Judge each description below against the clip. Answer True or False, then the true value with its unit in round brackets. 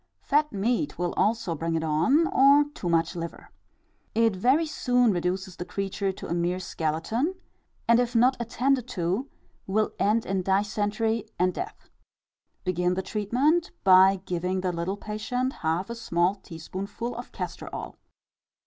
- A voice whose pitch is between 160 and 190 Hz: False (200 Hz)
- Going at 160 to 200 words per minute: False (150 wpm)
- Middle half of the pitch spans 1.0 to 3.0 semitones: False (5.2 semitones)